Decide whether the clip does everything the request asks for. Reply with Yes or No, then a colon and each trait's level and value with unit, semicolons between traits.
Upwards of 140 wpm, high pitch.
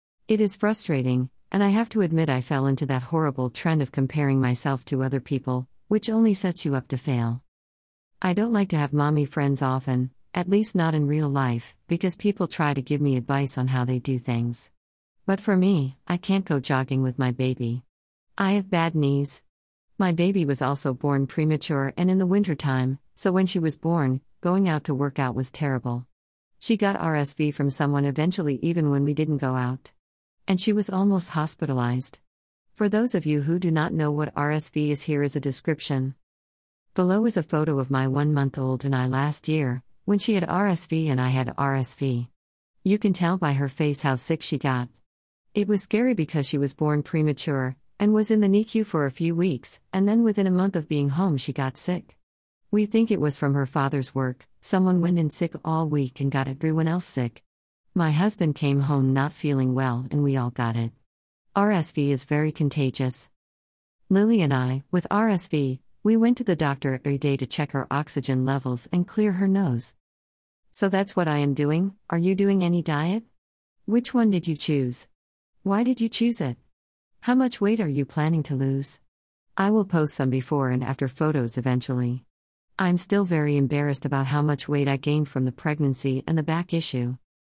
No: average, 200 wpm; medium, 145 Hz